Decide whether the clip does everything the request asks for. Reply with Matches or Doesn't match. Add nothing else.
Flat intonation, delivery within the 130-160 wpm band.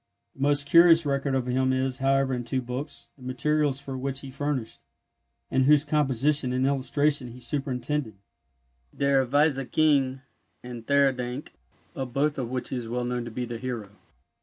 Doesn't match